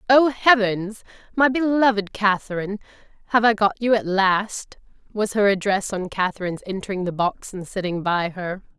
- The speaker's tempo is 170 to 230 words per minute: No, average, 155 wpm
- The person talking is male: No, female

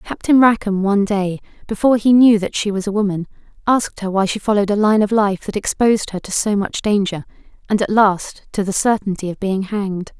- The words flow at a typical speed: No, fast, 220 wpm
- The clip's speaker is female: Yes, female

